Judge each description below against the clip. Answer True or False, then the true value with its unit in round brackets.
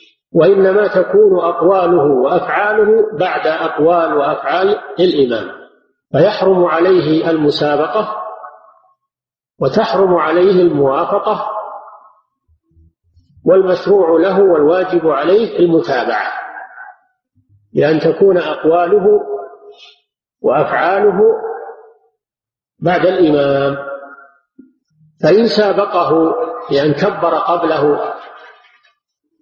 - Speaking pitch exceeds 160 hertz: True (190 Hz)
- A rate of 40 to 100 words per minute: True (65 wpm)